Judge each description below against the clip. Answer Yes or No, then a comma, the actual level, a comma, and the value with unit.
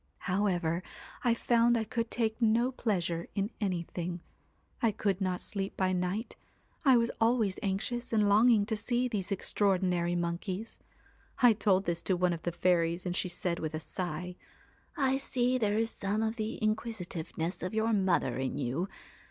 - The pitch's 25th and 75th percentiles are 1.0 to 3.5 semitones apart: No, average, 4.1 semitones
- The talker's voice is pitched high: Yes, high, 200 Hz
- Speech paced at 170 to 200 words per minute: Yes, average, 175 wpm